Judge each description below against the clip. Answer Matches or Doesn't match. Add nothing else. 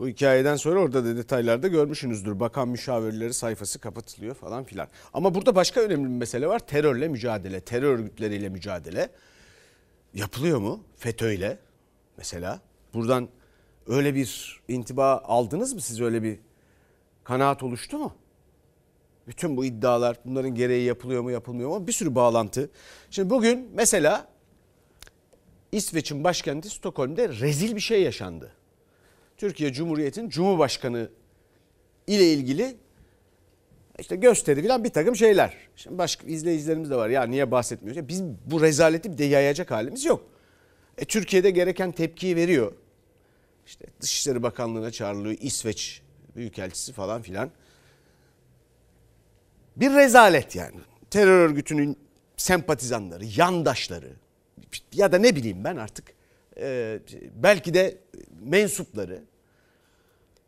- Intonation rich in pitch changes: Matches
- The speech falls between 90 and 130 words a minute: Matches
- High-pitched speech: Doesn't match